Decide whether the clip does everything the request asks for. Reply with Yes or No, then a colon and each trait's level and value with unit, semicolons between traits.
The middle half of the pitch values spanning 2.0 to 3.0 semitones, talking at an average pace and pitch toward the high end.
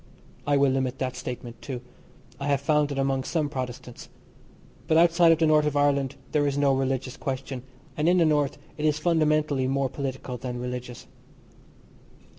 No: narrow, 2.6 semitones; average, 175 wpm; medium, 140 Hz